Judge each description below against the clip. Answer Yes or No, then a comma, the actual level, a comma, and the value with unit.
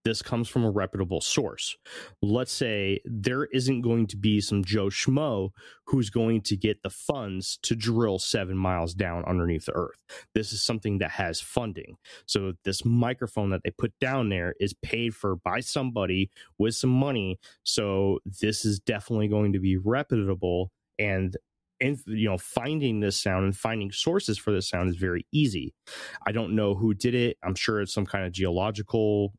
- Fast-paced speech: No, average, 180 wpm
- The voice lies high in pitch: No, low, 105 Hz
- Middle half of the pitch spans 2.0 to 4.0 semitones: Yes, average, 3.3 semitones